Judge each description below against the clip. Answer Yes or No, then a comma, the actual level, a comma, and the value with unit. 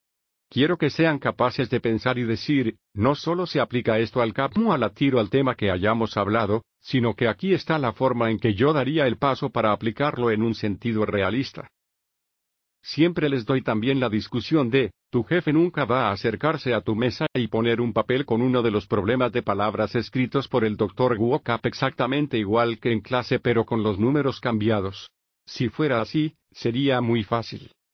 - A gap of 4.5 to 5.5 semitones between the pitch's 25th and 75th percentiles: No, average, 3.4 semitones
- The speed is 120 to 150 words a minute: No, average, 190 wpm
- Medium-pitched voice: No, low, 120 Hz